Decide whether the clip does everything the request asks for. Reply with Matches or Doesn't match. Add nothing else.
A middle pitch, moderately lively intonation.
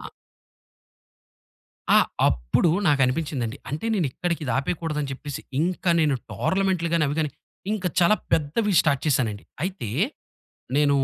Matches